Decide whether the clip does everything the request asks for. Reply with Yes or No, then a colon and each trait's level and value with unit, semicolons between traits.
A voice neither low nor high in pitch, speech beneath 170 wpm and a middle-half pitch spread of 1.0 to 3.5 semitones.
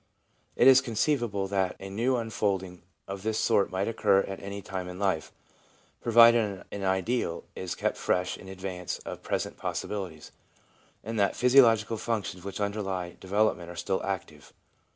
No: low, 100 Hz; average, 155 wpm; average, 2.9 semitones